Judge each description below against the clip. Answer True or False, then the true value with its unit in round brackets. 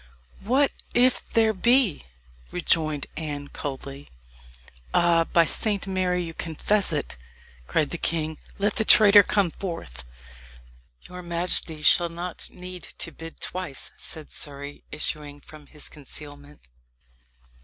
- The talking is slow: True (120 wpm)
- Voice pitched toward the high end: False (165 Hz)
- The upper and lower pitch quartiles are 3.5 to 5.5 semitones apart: True (4.0 semitones)